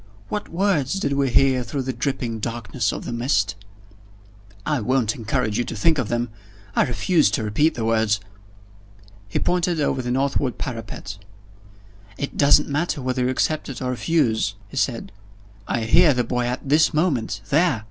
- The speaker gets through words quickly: No, average, 170 wpm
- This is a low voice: Yes, low, 130 Hz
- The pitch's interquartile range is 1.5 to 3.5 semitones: No, average, 4.2 semitones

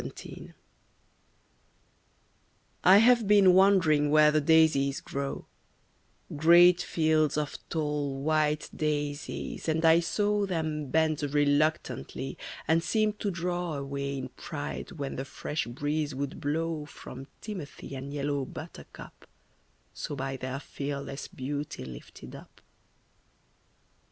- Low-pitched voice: No, medium, 150 Hz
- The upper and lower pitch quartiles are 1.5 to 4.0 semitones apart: Yes, average, 2.8 semitones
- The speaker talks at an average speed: No, slow, 115 wpm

